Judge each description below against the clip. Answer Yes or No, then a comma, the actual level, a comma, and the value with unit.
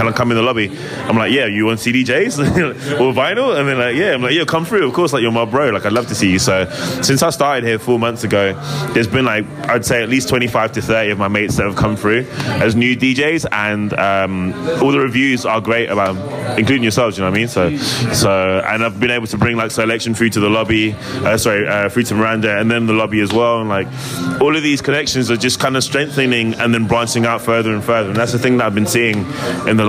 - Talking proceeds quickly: Yes, fast, 265 wpm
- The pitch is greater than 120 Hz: No, low, 115 Hz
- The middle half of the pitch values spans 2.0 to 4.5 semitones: Yes, average, 3.1 semitones